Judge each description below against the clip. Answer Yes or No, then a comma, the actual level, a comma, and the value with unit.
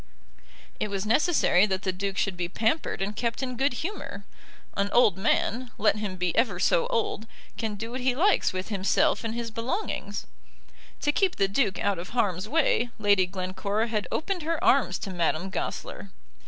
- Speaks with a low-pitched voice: No, high, 210 Hz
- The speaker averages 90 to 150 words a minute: No, average, 180 wpm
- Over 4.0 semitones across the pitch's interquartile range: Yes, average, 4.4 semitones